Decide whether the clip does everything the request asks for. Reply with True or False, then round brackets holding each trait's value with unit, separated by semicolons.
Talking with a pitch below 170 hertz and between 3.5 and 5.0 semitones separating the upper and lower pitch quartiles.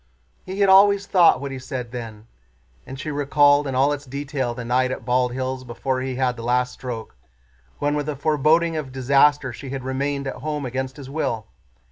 False (135 Hz; 2.4 semitones)